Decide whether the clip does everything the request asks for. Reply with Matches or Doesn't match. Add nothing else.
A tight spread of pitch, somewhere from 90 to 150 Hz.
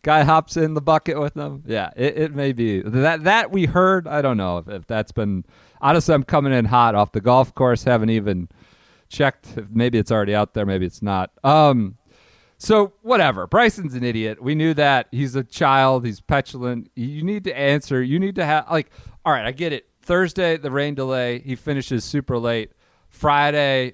Doesn't match